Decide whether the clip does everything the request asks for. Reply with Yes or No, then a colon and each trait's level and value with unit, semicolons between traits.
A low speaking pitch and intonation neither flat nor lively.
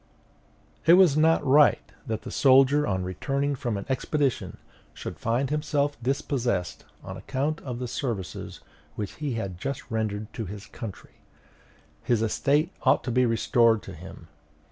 Yes: low, 125 Hz; average, 4.8 semitones